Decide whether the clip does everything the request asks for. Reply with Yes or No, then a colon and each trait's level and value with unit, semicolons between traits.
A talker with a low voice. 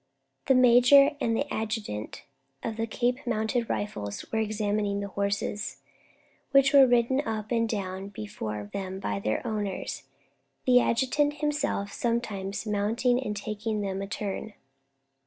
No: high, 215 Hz